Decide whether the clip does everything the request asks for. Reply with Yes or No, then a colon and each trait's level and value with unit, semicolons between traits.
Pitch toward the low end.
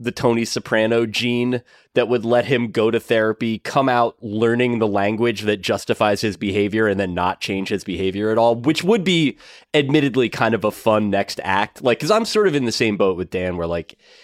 Yes: low, 115 Hz